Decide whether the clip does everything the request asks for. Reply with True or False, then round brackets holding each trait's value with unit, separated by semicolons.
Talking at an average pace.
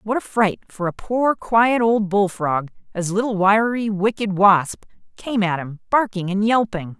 True (170 wpm)